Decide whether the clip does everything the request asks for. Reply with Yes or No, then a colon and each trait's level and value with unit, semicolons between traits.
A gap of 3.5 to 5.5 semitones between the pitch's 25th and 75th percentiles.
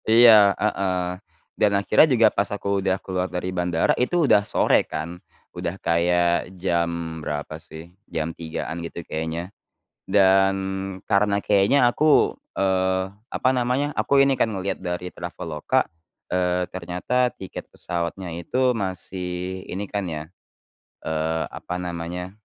No: average, 2.8 semitones